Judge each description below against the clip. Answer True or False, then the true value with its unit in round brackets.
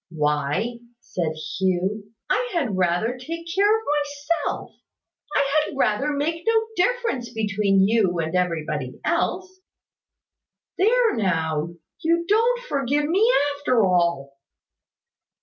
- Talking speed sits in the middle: False (115 wpm)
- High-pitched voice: True (230 Hz)